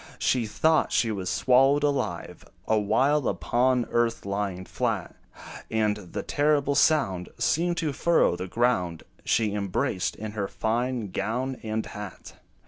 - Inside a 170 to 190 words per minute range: No, slow, 135 wpm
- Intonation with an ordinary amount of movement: Yes, average, 4.7 semitones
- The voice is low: Yes, low, 115 Hz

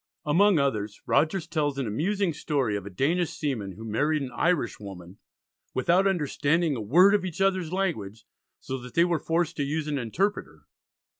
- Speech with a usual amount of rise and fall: No, wide, 6.6 semitones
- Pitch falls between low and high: Yes, medium, 150 Hz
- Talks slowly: No, average, 175 wpm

